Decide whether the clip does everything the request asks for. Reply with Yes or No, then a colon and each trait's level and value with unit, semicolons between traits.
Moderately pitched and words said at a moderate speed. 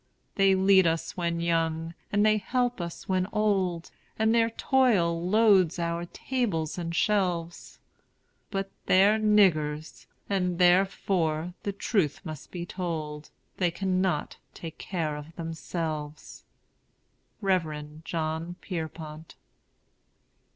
No: medium, 175 Hz; slow, 110 wpm